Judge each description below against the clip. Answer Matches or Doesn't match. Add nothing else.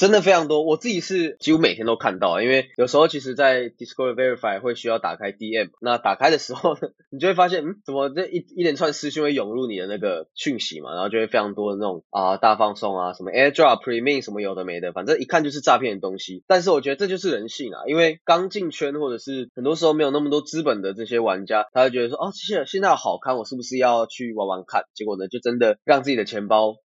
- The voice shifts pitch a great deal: Matches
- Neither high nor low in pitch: Doesn't match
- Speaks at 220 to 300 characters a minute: Doesn't match